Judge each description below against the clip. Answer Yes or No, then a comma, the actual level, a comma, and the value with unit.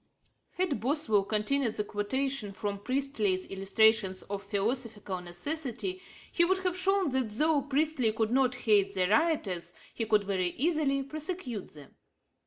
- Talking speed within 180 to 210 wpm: No, average, 140 wpm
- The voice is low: No, high, 230 Hz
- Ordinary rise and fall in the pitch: No, wide, 6.3 semitones